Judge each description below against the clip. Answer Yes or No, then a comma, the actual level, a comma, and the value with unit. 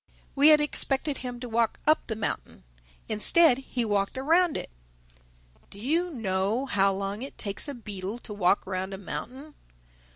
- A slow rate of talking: No, average, 165 wpm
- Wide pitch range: Yes, wide, 5.9 semitones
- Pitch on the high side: Yes, high, 235 Hz